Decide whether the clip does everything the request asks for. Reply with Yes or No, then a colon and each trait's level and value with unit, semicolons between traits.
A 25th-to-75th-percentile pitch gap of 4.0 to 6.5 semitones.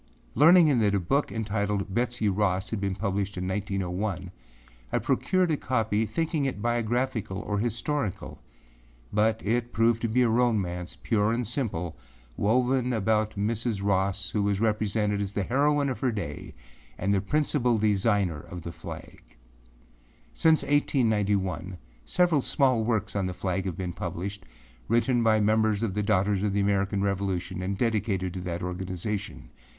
No: average, 3.4 semitones